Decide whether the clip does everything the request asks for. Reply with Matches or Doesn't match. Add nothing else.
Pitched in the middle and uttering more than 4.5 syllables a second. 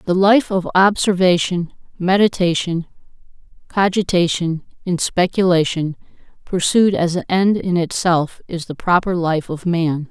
Doesn't match